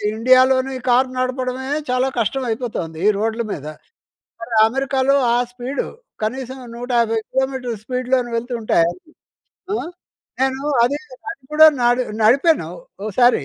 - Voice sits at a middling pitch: No, very high, 255 Hz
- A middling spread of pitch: No, narrow, 2.0 semitones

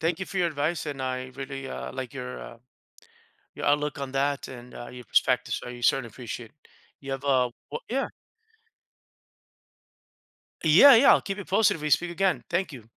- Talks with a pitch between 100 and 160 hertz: Yes, medium, 140 Hz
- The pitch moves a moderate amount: Yes, average, 4.8 semitones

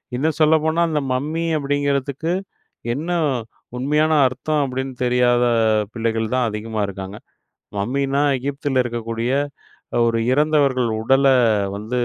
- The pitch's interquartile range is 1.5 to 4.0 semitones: Yes, average, 3.7 semitones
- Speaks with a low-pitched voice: Yes, low, 130 Hz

